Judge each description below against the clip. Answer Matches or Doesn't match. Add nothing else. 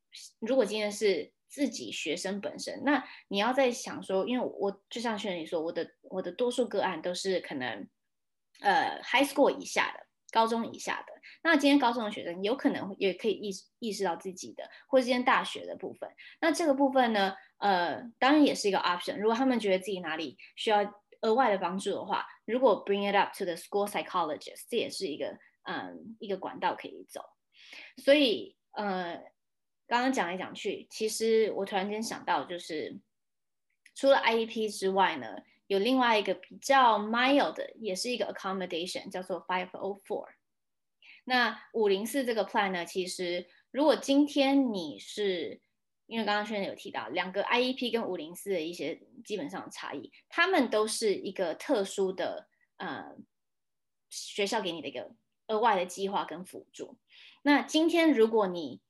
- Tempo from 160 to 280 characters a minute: Doesn't match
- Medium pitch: Doesn't match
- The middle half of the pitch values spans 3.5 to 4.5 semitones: Doesn't match